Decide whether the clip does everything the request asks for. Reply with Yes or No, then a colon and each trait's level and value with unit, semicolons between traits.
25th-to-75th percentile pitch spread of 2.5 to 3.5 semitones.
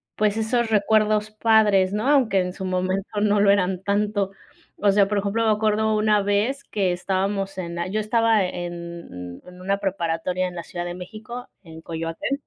Yes: average, 2.9 semitones